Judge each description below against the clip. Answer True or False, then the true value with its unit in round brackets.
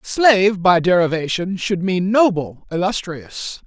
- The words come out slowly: True (115 wpm)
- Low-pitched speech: False (185 Hz)